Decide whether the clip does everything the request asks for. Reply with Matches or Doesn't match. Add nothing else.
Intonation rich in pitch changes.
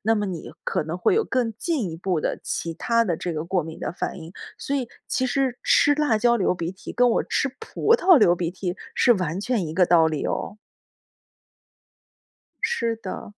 Matches